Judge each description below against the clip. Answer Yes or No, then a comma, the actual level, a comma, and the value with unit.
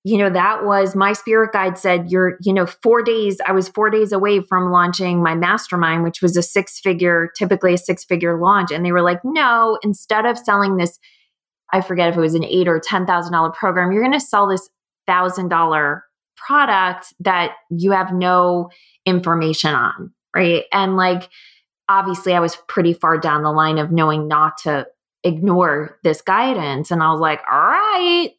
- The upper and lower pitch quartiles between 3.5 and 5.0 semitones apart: No, average, 2.8 semitones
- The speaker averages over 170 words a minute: Yes, average, 185 wpm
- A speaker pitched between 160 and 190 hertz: Yes, medium, 185 Hz